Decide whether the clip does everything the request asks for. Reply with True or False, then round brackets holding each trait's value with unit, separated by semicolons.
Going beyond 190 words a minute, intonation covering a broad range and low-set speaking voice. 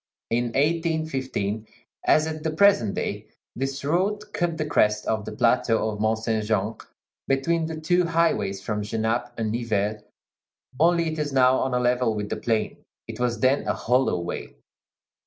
False (170 wpm; 6.4 semitones; 125 Hz)